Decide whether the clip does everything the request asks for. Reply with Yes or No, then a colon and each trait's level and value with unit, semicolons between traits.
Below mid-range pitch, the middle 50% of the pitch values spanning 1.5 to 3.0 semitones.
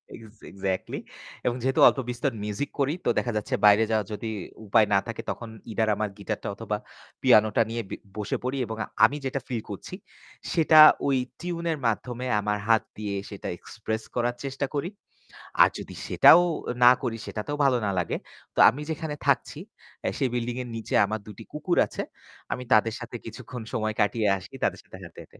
No: low, 115 Hz; average, 3.6 semitones